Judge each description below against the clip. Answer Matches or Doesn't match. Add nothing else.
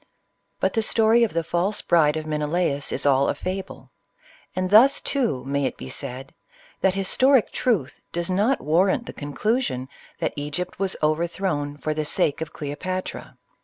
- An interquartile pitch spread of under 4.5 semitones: Doesn't match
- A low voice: Doesn't match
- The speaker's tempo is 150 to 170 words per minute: Matches